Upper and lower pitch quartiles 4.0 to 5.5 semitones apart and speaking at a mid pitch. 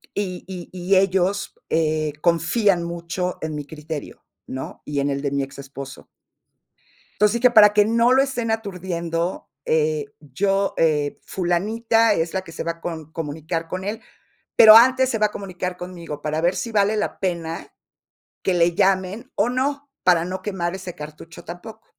Yes: average, 4.3 semitones; medium, 180 Hz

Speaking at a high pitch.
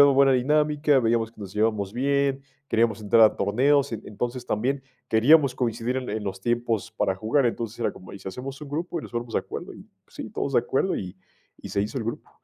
No: low, 120 Hz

